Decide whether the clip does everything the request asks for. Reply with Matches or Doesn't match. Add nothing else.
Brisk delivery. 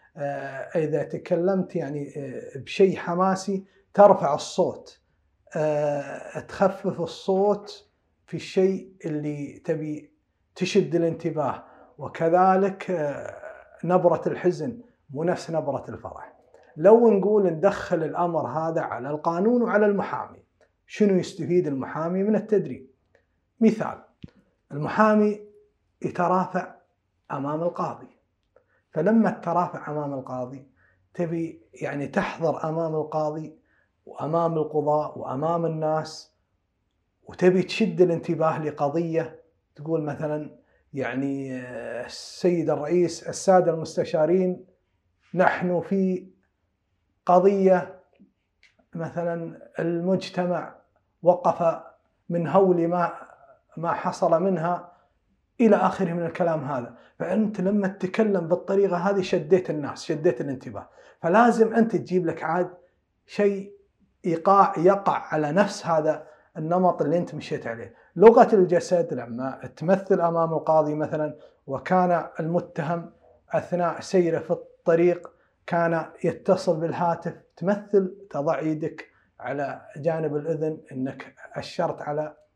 Doesn't match